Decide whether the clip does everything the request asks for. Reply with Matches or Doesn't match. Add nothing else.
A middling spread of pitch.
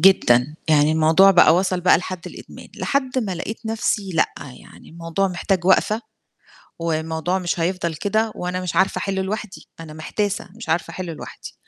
Matches